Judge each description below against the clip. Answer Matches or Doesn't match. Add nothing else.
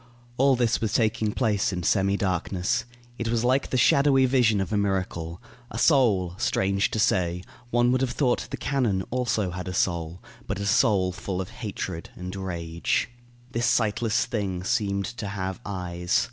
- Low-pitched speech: Matches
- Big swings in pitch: Doesn't match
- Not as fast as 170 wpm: Doesn't match